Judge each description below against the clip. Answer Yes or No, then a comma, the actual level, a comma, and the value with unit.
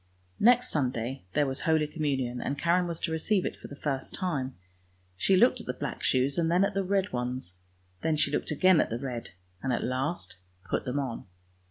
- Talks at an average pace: No, fast, 215 wpm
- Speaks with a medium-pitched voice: Yes, medium, 145 Hz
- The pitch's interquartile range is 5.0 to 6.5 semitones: Yes, wide, 5.4 semitones